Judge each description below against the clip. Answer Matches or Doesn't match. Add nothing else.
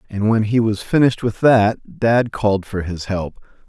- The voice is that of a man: Matches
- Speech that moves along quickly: Doesn't match